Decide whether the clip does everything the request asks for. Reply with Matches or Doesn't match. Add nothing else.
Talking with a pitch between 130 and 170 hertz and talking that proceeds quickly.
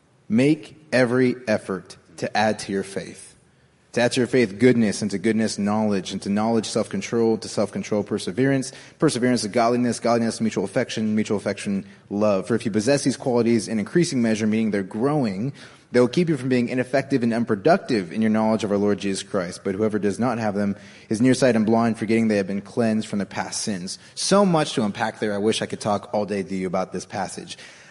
Doesn't match